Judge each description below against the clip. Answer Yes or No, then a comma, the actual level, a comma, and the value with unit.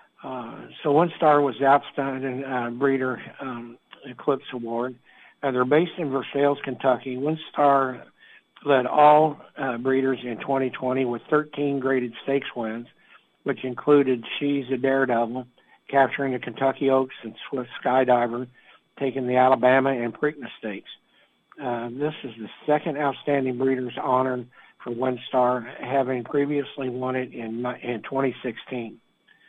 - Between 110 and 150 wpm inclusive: Yes, average, 140 wpm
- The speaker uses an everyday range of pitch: No, narrow, 2.0 semitones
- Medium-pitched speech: No, low, 130 Hz